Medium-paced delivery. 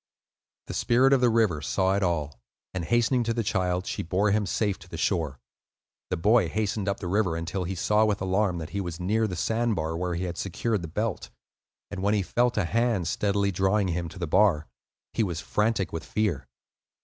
No: fast, 215 wpm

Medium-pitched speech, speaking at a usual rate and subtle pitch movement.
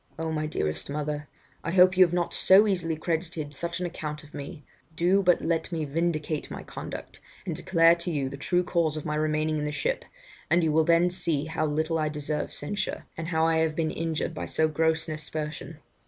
No: medium, 160 Hz; fast, 215 wpm; narrow, 2.0 semitones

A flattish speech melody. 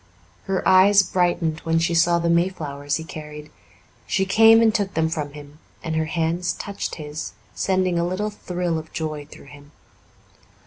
No: average, 3.3 semitones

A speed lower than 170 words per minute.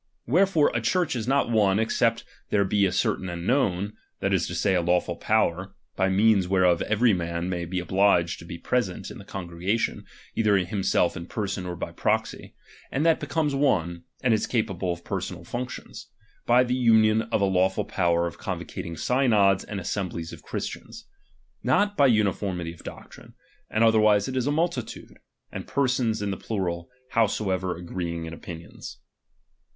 No: average, 175 wpm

